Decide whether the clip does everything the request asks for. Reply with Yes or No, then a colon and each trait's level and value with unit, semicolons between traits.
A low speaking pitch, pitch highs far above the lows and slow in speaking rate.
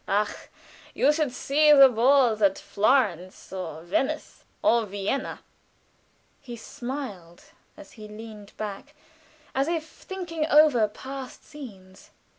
No: high, 240 Hz; wide, 5.8 semitones; slow, 115 wpm